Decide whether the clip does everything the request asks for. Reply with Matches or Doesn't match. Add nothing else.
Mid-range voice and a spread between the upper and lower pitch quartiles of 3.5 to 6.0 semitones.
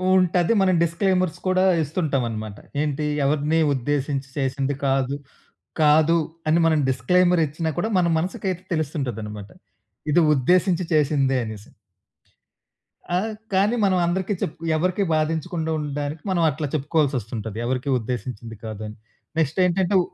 Matches